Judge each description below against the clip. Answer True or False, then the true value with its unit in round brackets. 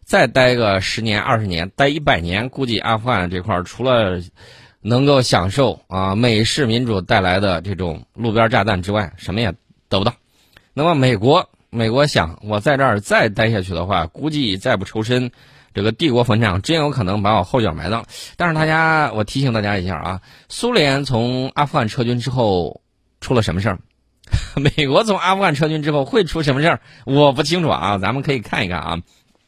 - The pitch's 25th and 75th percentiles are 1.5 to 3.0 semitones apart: False (5.4 semitones)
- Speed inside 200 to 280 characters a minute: False (295 characters per minute)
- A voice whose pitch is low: True (115 Hz)